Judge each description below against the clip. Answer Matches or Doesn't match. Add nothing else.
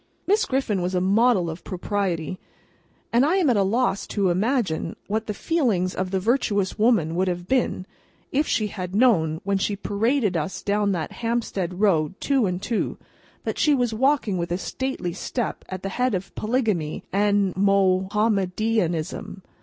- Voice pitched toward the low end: Doesn't match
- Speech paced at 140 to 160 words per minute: Doesn't match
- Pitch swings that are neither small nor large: Matches